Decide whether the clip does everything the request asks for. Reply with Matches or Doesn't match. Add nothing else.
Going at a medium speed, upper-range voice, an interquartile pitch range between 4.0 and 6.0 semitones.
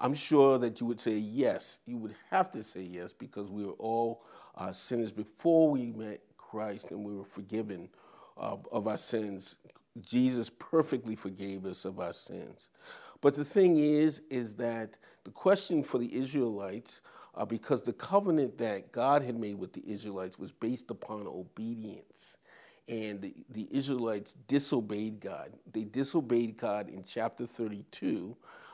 Doesn't match